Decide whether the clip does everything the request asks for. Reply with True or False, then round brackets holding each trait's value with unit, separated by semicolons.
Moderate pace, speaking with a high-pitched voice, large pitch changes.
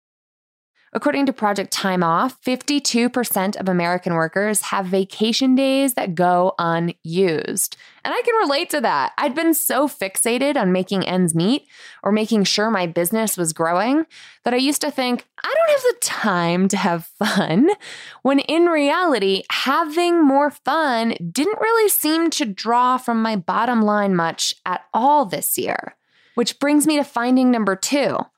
True (160 wpm; 240 Hz; 7.0 semitones)